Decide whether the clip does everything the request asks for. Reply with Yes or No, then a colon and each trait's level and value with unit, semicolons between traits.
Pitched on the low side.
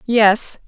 No: high, 220 Hz